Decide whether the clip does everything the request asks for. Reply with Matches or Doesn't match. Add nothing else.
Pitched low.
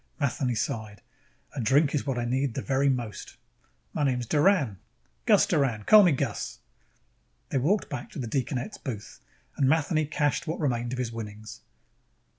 Matches